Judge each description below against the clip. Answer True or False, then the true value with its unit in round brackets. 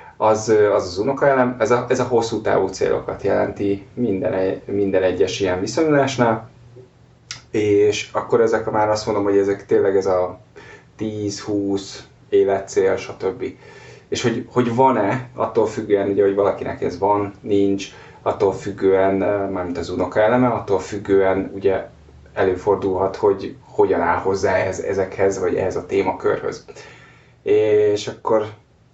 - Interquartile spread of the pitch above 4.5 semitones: True (5.6 semitones)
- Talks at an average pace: True (135 wpm)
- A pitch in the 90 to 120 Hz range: True (110 Hz)